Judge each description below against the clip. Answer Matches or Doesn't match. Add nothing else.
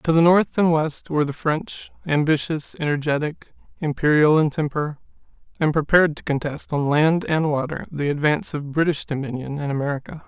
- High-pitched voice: Doesn't match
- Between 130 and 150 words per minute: Doesn't match